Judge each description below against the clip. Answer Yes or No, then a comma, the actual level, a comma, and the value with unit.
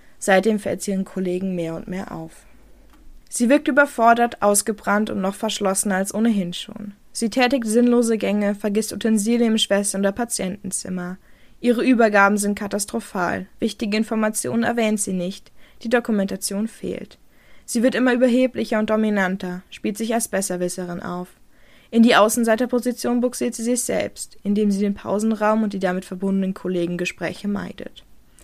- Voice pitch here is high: Yes, high, 210 Hz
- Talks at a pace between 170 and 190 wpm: No, average, 150 wpm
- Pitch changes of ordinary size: Yes, average, 3.3 semitones